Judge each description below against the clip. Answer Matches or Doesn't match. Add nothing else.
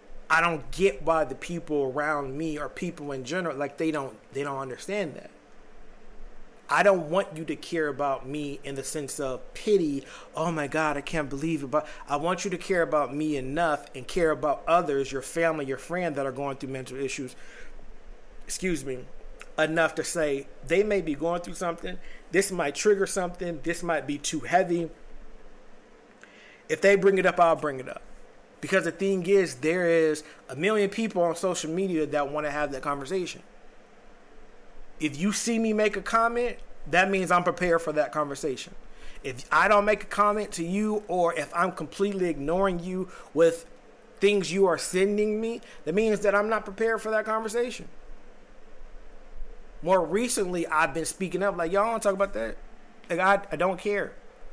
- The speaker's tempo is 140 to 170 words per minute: Doesn't match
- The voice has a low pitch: Doesn't match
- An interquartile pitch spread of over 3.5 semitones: Matches